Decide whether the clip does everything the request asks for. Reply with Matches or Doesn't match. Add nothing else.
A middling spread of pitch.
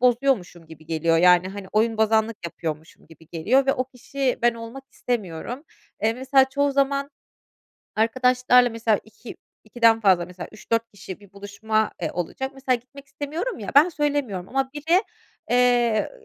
Matches